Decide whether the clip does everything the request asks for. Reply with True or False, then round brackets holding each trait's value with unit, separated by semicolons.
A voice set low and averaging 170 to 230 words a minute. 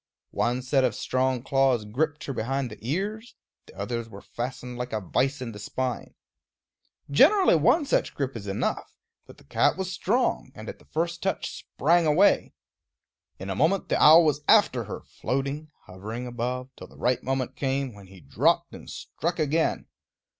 True (130 Hz; 175 wpm)